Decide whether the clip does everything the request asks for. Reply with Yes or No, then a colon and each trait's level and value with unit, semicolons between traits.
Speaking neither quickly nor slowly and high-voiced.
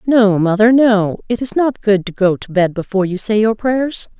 No: fast, 230 wpm; high, 210 Hz